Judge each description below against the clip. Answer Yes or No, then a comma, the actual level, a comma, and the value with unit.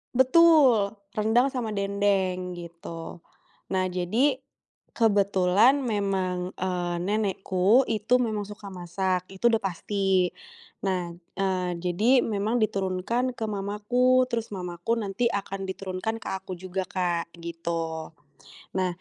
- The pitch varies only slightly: No, average, 3.4 semitones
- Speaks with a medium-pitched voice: No, high, 195 Hz